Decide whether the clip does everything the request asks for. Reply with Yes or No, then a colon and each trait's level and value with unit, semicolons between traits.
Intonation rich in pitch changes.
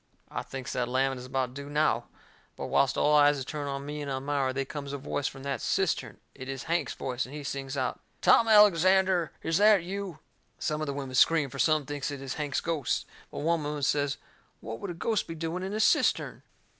No: average, 3.5 semitones